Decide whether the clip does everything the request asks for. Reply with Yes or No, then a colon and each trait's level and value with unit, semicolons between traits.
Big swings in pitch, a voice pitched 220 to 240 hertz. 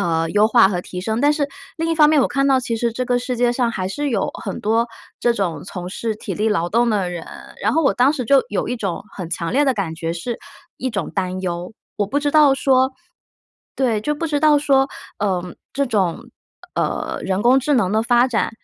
Yes: wide, 5.7 semitones; high, 235 Hz